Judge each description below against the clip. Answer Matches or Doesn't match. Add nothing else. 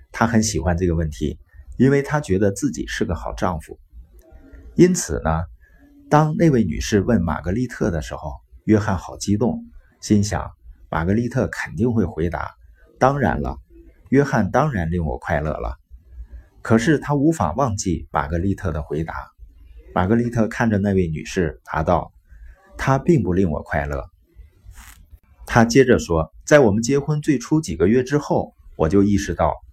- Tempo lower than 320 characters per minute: Matches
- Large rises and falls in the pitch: Matches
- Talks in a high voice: Doesn't match